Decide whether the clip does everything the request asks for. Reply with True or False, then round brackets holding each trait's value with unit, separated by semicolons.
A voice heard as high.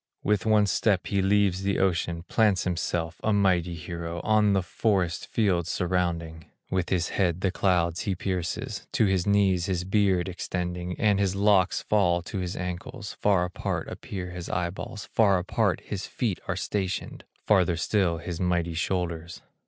False (90 Hz)